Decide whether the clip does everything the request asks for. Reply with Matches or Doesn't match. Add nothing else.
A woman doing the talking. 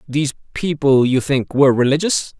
Doesn't match